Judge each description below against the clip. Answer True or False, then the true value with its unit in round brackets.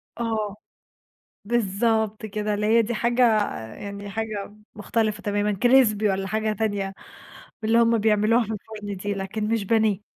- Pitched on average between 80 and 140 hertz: False (215 Hz)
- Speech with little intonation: True (1.5 semitones)